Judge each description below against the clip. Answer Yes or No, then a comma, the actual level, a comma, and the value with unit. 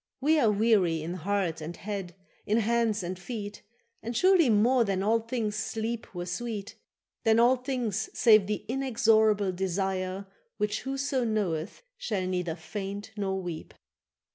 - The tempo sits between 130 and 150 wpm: Yes, average, 145 wpm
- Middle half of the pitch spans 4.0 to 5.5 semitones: No, average, 3.6 semitones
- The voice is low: No, high, 210 Hz